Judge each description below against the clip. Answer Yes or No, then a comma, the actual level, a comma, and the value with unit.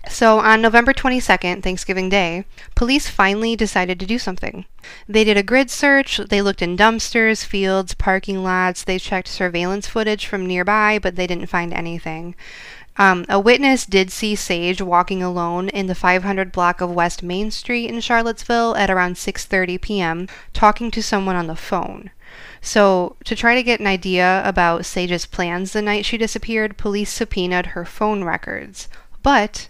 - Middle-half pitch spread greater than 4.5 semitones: No, average, 3.3 semitones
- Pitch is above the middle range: Yes, high, 195 Hz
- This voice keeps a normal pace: Yes, average, 170 wpm